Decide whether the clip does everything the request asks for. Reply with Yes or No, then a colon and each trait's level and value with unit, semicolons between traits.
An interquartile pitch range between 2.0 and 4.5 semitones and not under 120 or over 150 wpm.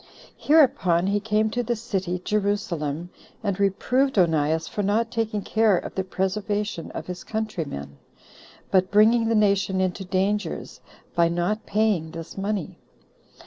Yes: average, 3.3 semitones; average, 140 wpm